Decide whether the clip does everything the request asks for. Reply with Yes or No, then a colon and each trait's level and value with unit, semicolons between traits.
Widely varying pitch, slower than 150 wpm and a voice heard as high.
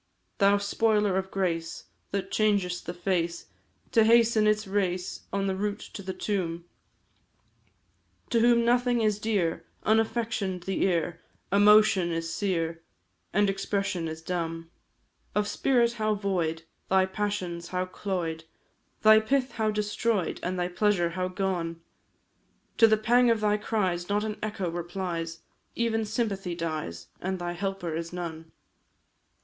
No: average, 3.6 semitones; average, 140 wpm; high, 195 Hz